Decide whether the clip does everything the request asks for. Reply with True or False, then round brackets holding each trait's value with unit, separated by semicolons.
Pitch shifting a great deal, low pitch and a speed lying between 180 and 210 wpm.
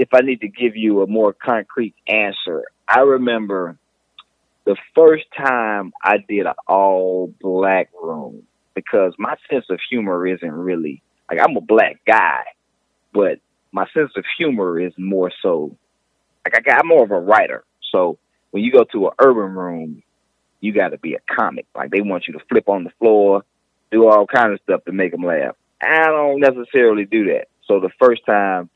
True (8.7 semitones; 110 Hz; 185 wpm)